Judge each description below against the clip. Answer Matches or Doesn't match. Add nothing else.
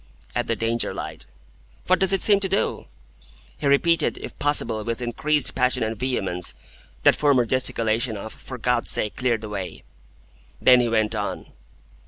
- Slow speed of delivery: Doesn't match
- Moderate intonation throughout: Matches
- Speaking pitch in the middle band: Doesn't match